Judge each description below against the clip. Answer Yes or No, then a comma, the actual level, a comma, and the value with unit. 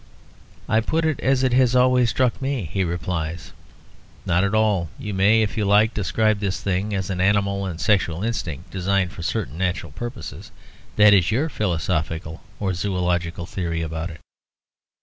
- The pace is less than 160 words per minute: No, average, 170 wpm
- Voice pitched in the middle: No, low, 100 Hz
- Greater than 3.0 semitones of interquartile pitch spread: Yes, average, 3.9 semitones